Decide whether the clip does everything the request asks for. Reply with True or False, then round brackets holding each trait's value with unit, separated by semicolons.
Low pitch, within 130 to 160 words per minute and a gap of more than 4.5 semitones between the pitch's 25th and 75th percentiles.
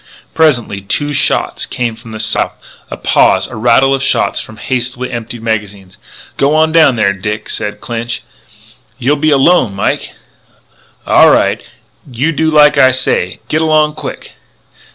True (125 Hz; 155 wpm; 5.1 semitones)